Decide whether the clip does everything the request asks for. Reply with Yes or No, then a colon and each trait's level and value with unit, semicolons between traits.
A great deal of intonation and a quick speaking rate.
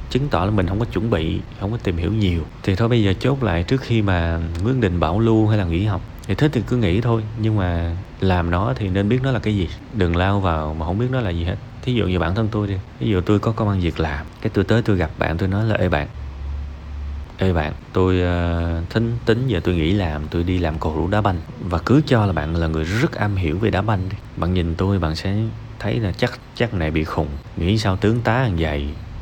No: average, 4.8 semitones; fast, 270 wpm